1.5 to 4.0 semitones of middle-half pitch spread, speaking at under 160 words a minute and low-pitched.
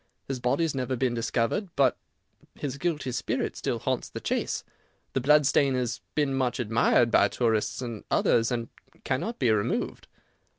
No: average, 2.8 semitones; average, 165 wpm; low, 130 Hz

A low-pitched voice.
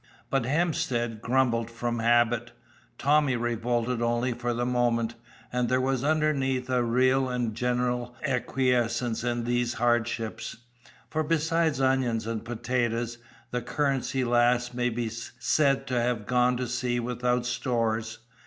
Yes: low, 120 Hz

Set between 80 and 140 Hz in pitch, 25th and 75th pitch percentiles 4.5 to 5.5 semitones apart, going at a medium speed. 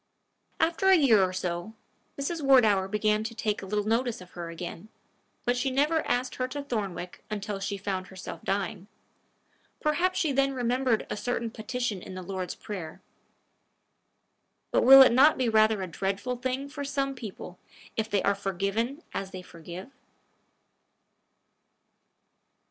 No: high, 220 Hz; average, 5.2 semitones; average, 155 wpm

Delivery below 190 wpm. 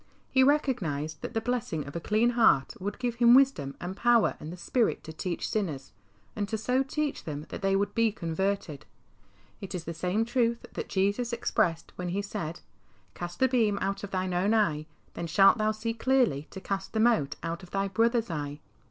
No: fast, 205 wpm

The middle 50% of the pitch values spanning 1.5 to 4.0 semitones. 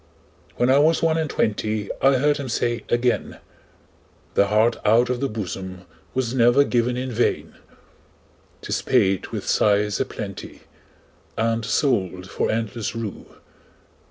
Yes: average, 3.6 semitones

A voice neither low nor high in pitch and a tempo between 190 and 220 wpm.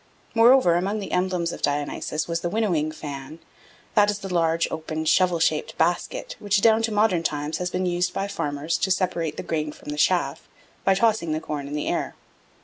Yes: medium, 170 Hz; average, 200 wpm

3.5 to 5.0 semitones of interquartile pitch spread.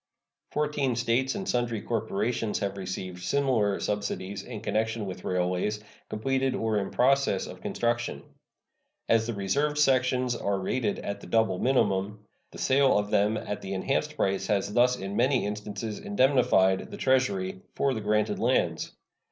Yes: average, 4.1 semitones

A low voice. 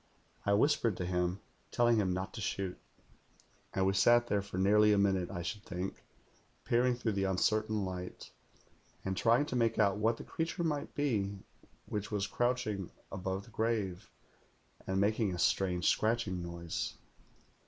Yes: low, 100 Hz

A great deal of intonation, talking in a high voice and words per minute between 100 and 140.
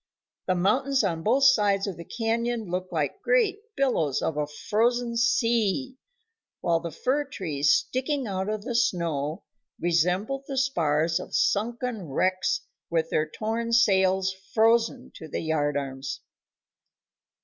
Yes: wide, 6.2 semitones; high, 200 Hz; slow, 135 wpm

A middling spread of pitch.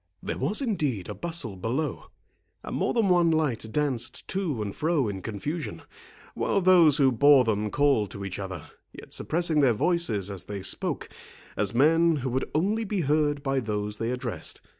No: wide, 7.4 semitones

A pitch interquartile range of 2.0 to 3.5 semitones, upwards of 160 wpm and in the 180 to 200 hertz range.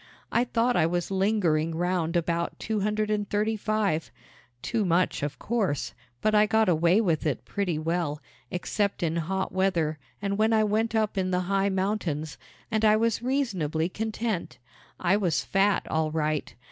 No: average, 4.3 semitones; average, 170 wpm; high, 190 Hz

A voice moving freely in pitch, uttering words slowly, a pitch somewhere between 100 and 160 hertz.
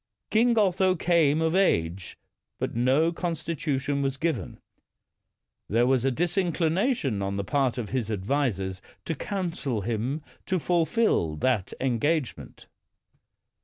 Yes: wide, 6.6 semitones; slow, 120 wpm; medium, 140 Hz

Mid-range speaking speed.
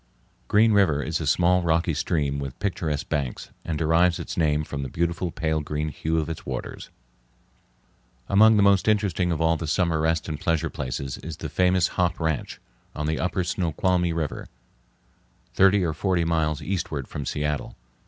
Yes: average, 175 wpm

